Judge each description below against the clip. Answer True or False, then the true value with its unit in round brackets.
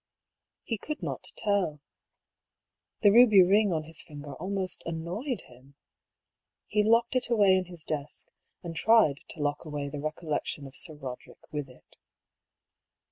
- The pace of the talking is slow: False (145 wpm)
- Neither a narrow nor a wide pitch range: False (5.8 semitones)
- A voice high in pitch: False (170 Hz)